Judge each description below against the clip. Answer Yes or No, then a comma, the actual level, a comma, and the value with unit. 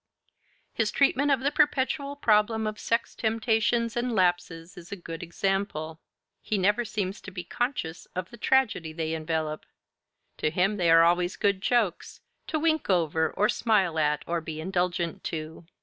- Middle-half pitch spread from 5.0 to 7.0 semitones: Yes, wide, 5.6 semitones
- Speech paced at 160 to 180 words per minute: Yes, average, 165 wpm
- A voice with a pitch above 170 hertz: Yes, high, 190 Hz